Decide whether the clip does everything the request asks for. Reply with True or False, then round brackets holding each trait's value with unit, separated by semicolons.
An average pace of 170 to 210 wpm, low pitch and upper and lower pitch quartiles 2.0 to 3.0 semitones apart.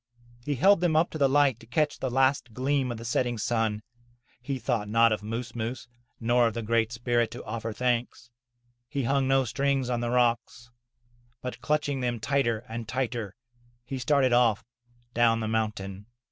True (180 wpm; 120 Hz; 2.7 semitones)